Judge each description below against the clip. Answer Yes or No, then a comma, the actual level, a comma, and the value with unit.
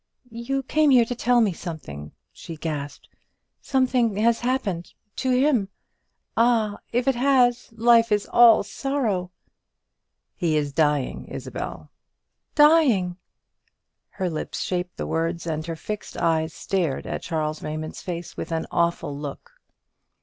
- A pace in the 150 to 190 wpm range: No, slow, 135 wpm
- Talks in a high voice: Yes, high, 195 Hz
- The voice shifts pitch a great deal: Yes, wide, 6.9 semitones